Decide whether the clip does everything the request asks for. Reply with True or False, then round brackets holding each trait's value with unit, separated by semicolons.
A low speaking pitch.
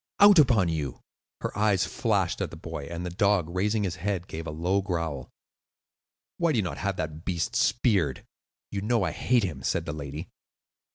True (90 Hz)